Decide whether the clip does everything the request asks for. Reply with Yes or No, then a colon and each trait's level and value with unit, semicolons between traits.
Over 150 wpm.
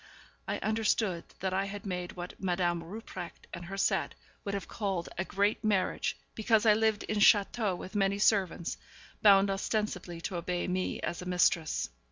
Yes: average, 170 wpm